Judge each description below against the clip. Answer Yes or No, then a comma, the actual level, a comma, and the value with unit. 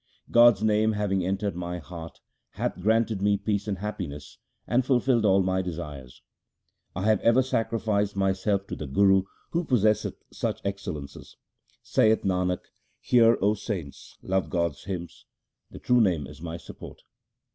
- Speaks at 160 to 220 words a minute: No, average, 145 wpm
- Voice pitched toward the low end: Yes, low, 100 Hz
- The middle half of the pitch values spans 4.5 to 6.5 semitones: No, average, 3.5 semitones